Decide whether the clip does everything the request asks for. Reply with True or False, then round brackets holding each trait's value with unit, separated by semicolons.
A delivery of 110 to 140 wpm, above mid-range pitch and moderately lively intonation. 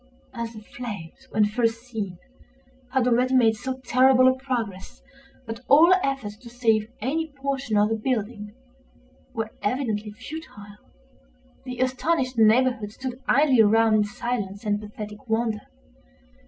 True (135 wpm; 235 Hz; 3.5 semitones)